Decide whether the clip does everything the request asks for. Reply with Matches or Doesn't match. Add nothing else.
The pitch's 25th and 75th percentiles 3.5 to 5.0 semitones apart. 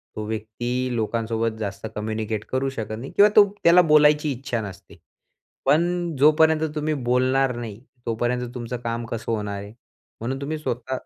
Matches